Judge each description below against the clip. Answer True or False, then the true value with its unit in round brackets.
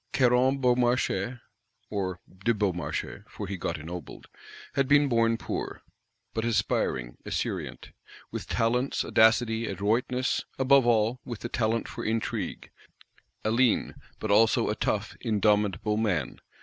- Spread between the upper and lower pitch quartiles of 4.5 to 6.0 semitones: False (3.2 semitones)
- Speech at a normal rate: False (125 wpm)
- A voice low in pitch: True (115 Hz)